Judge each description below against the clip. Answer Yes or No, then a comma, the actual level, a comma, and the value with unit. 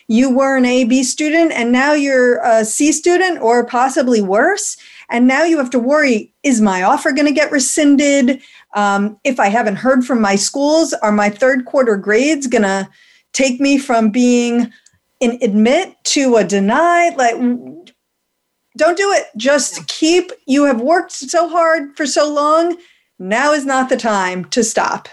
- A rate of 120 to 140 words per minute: No, average, 175 wpm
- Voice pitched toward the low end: No, very high, 265 Hz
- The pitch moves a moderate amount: Yes, average, 4.7 semitones